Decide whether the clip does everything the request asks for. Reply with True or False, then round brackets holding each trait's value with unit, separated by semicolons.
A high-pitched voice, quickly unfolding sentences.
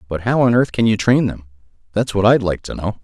False (105 Hz; 275 wpm)